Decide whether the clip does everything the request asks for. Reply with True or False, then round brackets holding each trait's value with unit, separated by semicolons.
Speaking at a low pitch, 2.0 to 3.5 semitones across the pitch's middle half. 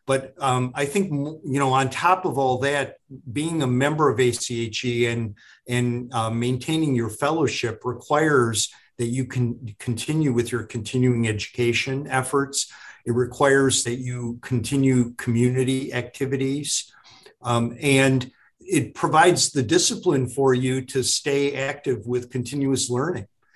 True (130 Hz; 2.4 semitones)